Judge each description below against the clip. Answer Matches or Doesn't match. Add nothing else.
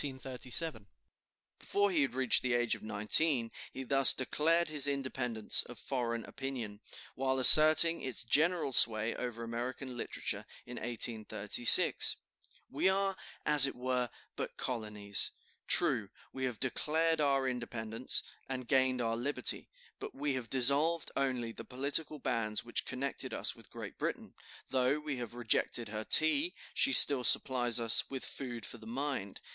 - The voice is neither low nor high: Doesn't match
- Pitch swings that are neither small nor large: Matches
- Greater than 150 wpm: Doesn't match